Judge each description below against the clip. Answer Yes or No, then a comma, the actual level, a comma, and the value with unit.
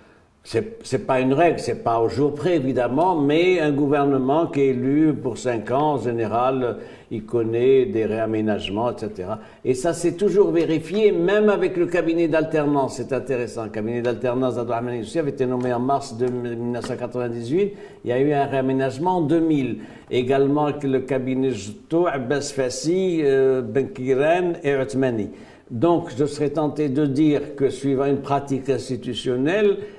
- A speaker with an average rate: Yes, average, 160 wpm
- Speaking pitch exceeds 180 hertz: No, low, 135 Hz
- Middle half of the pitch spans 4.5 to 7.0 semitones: No, average, 3.9 semitones